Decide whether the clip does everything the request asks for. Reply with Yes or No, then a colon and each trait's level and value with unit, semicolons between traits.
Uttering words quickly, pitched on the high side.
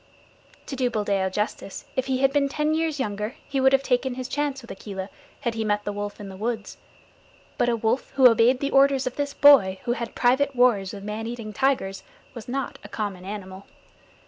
Yes: fast, 210 wpm; high, 240 Hz